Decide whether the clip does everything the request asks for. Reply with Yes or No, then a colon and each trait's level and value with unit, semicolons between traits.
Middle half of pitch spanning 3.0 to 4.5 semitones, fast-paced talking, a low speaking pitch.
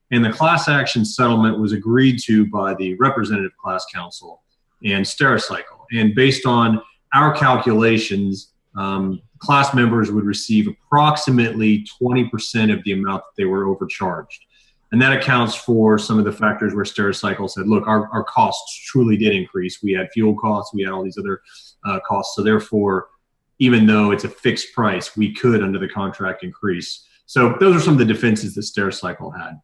No: average, 3.4 semitones; average, 175 wpm; low, 110 Hz